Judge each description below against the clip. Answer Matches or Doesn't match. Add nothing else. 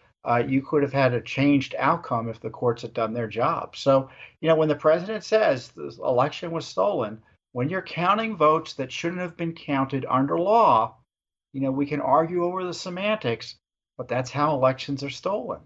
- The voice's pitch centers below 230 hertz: Matches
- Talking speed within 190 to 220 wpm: Matches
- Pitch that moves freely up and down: Doesn't match